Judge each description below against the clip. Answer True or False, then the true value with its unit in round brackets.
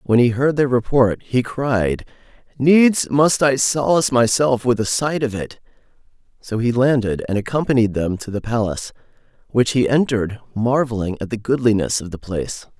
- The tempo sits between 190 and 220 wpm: False (170 wpm)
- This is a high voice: False (120 Hz)